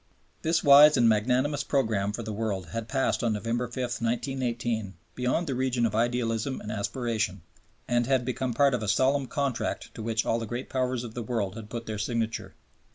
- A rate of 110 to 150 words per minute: No, average, 195 wpm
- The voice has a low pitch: Yes, low, 120 Hz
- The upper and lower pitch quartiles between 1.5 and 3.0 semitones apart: Yes, average, 2.7 semitones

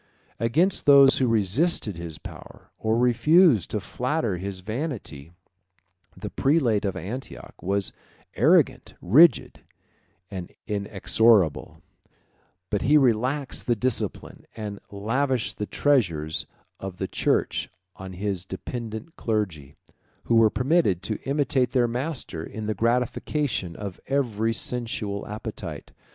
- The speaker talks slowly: Yes, slow, 115 wpm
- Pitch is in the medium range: No, low, 110 Hz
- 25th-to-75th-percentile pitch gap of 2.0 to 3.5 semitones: No, average, 4.8 semitones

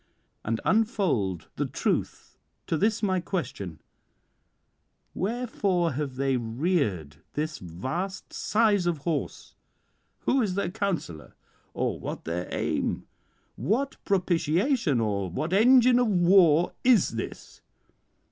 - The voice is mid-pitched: Yes, medium, 175 Hz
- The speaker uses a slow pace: Yes, slow, 110 wpm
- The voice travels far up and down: Yes, wide, 8.5 semitones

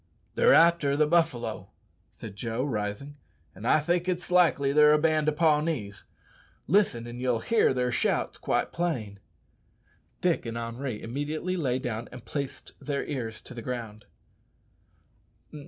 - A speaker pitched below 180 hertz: Yes, medium, 140 Hz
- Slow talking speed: No, average, 145 wpm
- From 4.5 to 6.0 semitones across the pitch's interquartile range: Yes, average, 5.2 semitones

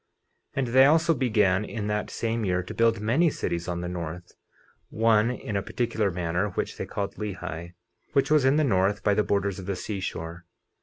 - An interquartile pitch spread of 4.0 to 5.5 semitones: Yes, average, 4.3 semitones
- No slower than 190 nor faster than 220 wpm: Yes, average, 200 wpm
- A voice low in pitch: Yes, low, 105 Hz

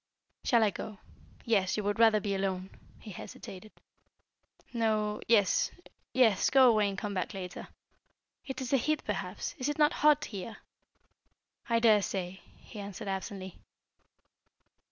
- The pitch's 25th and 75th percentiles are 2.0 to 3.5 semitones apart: Yes, average, 3.1 semitones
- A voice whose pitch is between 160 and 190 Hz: No, high, 210 Hz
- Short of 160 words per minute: Yes, average, 145 wpm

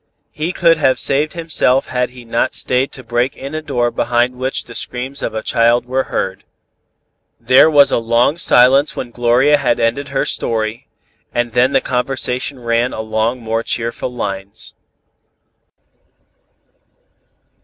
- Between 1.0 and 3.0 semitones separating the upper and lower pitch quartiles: Yes, narrow, 2.5 semitones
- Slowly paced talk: No, average, 145 wpm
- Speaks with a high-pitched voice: No, low, 125 Hz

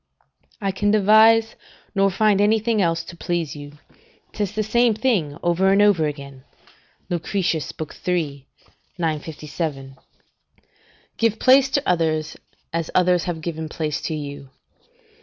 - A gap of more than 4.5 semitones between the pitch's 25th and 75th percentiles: Yes, average, 5.2 semitones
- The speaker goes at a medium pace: No, slow, 125 wpm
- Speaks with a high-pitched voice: No, medium, 175 Hz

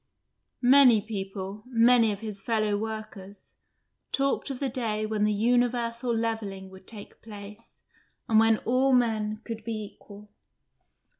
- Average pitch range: No, narrow, 2.1 semitones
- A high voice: Yes, high, 220 Hz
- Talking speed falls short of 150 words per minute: Yes, slow, 135 wpm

